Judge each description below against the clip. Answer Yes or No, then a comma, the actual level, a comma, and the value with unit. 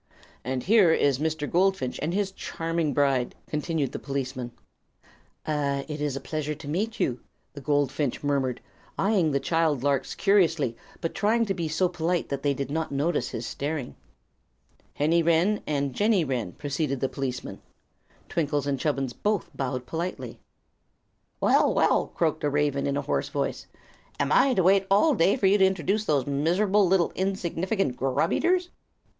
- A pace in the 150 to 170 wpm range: Yes, average, 160 wpm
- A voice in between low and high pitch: Yes, medium, 150 Hz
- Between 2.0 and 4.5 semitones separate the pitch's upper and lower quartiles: No, average, 5.0 semitones